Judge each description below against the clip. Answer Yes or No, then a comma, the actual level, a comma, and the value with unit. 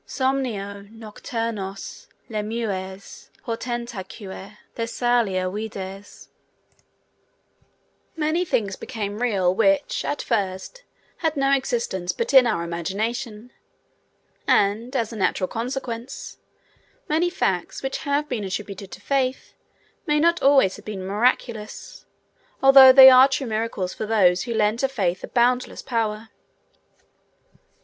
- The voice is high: Yes, high, 225 Hz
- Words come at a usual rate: No, slow, 115 wpm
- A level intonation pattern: No, average, 4.8 semitones